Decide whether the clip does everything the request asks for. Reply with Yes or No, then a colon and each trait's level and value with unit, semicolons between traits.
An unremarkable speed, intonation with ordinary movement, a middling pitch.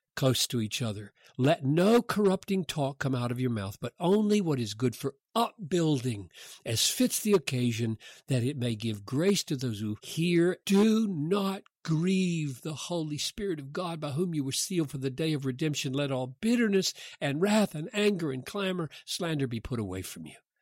No: average, 190 wpm; wide, 6.6 semitones; medium, 150 Hz